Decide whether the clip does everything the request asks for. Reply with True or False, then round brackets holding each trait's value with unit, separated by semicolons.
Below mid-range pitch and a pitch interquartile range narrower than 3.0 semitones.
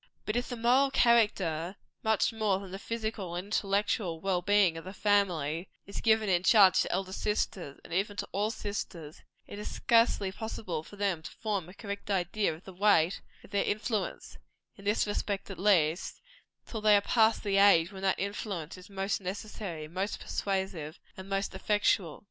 False (195 Hz; 2.6 semitones)